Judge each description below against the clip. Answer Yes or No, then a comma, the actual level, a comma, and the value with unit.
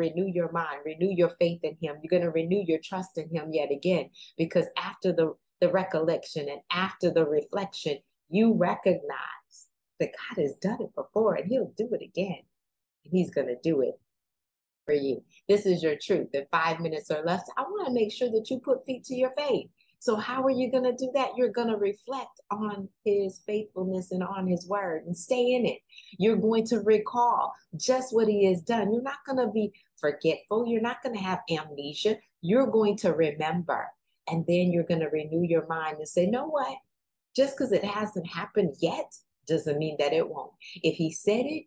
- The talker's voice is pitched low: No, high, 190 Hz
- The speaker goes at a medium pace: No, fast, 210 wpm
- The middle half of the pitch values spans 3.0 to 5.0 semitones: No, wide, 5.6 semitones